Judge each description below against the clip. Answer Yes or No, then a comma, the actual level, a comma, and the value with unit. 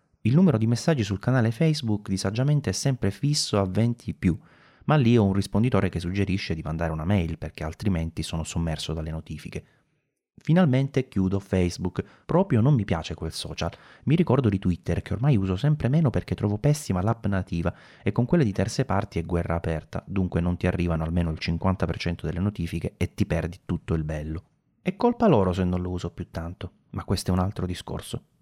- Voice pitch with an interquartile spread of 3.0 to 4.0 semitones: No, wide, 5.6 semitones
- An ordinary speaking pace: No, fast, 195 wpm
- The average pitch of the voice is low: Yes, very low, 95 Hz